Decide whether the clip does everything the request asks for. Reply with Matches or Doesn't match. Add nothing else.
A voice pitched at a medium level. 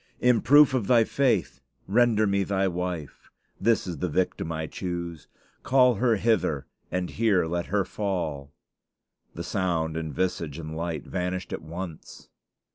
Doesn't match